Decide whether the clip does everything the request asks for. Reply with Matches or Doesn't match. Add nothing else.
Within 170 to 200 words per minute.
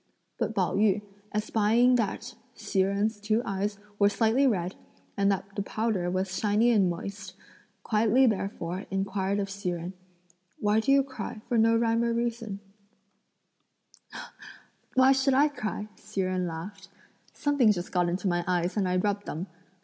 Doesn't match